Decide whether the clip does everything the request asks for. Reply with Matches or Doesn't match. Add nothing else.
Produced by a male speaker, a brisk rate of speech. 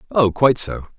Doesn't match